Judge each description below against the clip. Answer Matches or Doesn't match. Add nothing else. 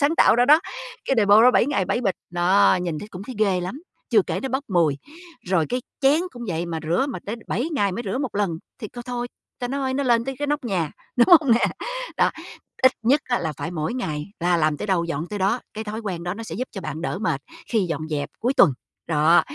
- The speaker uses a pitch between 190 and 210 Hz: Matches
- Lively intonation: Matches